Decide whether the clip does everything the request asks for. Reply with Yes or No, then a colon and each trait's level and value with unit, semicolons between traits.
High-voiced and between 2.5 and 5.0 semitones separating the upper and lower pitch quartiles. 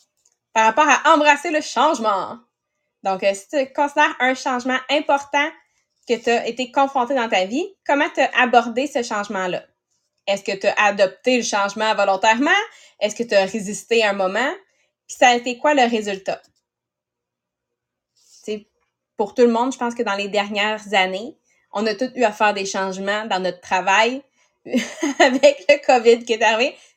No: high, 230 Hz; wide, 5.4 semitones